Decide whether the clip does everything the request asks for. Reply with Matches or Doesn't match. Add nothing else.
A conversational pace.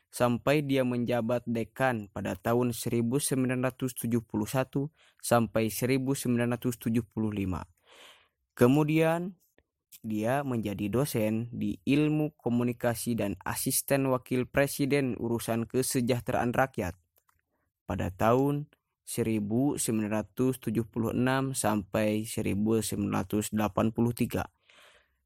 Doesn't match